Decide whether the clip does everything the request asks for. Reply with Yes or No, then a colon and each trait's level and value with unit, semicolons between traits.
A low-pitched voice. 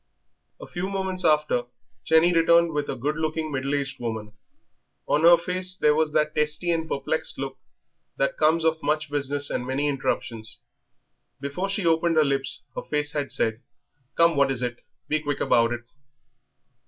No: medium, 150 Hz